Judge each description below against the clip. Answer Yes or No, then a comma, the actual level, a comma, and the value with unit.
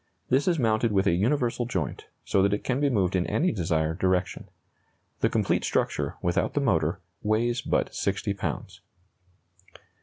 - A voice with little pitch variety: No, average, 5.0 semitones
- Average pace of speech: Yes, average, 160 wpm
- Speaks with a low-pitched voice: Yes, low, 105 Hz